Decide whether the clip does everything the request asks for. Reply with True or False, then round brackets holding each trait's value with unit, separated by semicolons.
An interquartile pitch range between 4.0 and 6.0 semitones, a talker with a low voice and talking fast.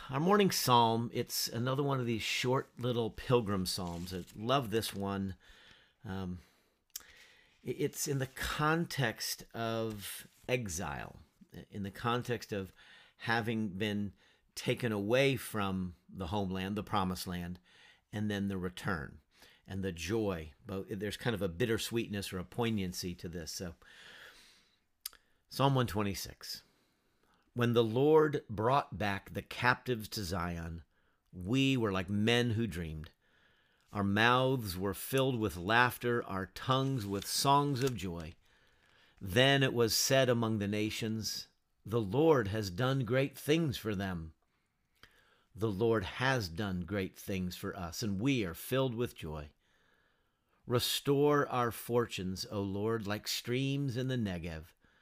False (4.6 semitones; 110 Hz; 135 wpm)